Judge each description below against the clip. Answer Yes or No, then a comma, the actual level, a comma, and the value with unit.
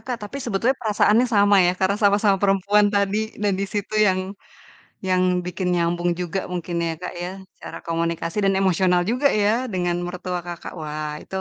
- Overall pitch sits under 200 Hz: Yes, high, 190 Hz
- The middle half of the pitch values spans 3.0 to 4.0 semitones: No, narrow, 2.6 semitones